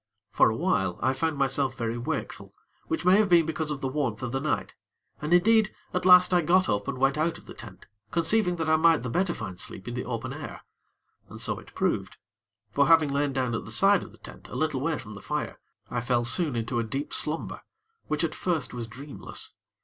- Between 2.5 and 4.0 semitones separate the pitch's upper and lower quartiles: No, average, 5.2 semitones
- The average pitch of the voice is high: No, medium, 145 Hz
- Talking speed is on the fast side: Yes, fast, 230 wpm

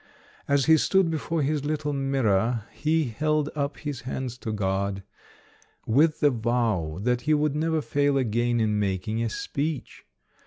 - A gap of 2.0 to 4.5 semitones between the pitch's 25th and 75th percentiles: No, average, 5.2 semitones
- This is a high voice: No, low, 135 Hz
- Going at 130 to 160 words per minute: Yes, average, 155 wpm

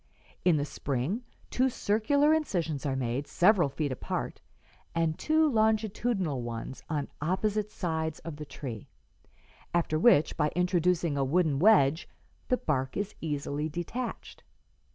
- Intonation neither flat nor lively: No, wide, 6.7 semitones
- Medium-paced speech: No, slow, 130 wpm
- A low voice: No, medium, 165 Hz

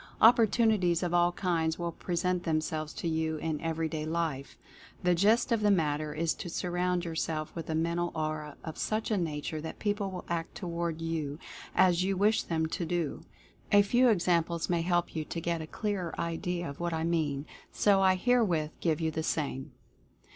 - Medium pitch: Yes, medium, 170 Hz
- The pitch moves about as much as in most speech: No, narrow, 2.3 semitones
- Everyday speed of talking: Yes, average, 190 wpm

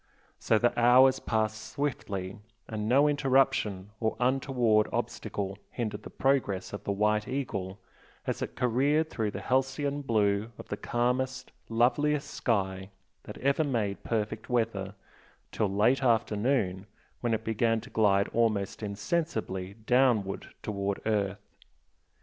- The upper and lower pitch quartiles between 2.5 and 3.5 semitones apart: No, average, 4.2 semitones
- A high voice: No, low, 110 Hz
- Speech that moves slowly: Yes, slow, 130 wpm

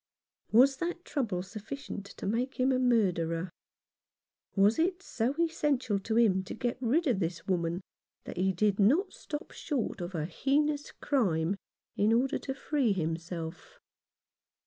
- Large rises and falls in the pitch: Yes, wide, 7.0 semitones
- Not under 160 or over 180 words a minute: No, average, 145 wpm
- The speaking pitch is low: No, high, 225 Hz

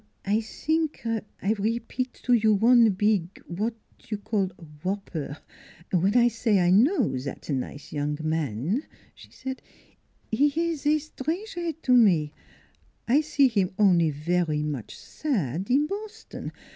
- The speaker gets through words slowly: No, average, 145 wpm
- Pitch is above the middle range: Yes, high, 215 Hz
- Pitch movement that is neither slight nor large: No, wide, 7.4 semitones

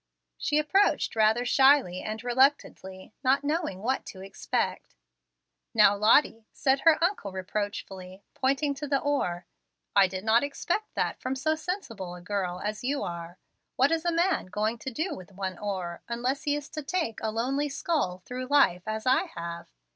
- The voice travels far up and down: Yes, wide, 6.9 semitones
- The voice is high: Yes, high, 235 Hz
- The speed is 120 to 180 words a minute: Yes, average, 170 wpm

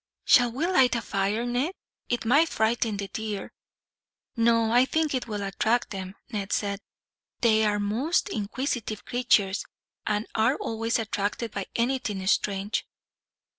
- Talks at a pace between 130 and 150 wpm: Yes, average, 140 wpm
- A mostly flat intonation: No, average, 3.1 semitones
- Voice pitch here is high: Yes, high, 225 Hz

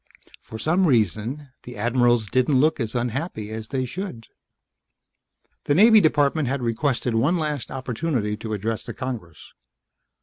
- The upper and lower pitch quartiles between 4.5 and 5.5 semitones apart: Yes, average, 4.8 semitones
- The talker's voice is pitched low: Yes, low, 125 Hz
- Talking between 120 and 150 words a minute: Yes, average, 140 wpm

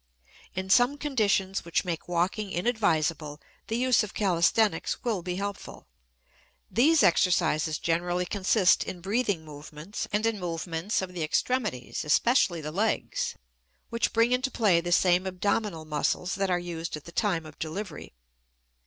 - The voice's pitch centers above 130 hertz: Yes, medium, 185 Hz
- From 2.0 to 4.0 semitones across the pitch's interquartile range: No, average, 4.5 semitones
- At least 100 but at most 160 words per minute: Yes, average, 145 wpm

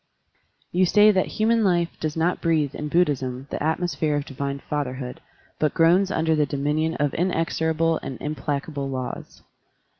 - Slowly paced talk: No, average, 160 wpm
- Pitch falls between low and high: Yes, medium, 155 Hz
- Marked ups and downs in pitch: No, average, 3.2 semitones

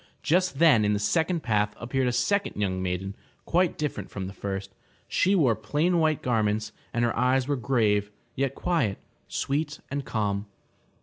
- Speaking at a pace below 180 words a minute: Yes, average, 170 wpm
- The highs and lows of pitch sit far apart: Yes, wide, 6.3 semitones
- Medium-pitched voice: No, low, 120 Hz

